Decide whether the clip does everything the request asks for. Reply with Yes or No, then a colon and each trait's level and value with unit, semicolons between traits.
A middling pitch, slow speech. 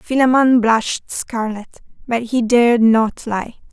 No: high, 235 Hz; slow, 130 wpm